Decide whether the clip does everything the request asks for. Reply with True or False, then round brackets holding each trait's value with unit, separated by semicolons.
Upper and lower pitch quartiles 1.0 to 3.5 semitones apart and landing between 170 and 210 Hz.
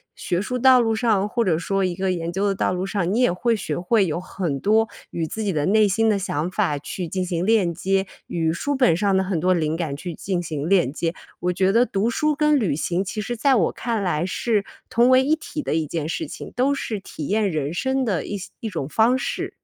False (4.7 semitones; 195 Hz)